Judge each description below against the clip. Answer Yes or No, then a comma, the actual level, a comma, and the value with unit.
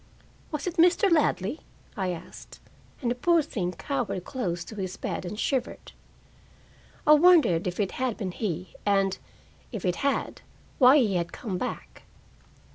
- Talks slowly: No, average, 155 wpm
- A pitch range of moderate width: No, wide, 7.6 semitones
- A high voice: Yes, high, 215 Hz